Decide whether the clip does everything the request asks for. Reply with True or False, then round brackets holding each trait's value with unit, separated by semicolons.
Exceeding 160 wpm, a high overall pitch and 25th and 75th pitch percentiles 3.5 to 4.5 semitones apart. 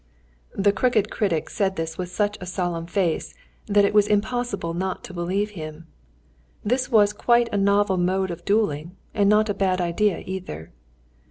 False (170 wpm; 195 Hz; 2.9 semitones)